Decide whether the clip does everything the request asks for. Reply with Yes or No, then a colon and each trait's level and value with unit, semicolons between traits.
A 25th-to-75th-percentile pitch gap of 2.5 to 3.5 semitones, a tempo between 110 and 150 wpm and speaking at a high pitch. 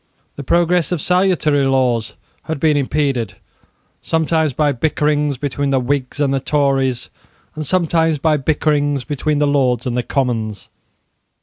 No: average, 2.8 semitones; average, 140 wpm; medium, 145 Hz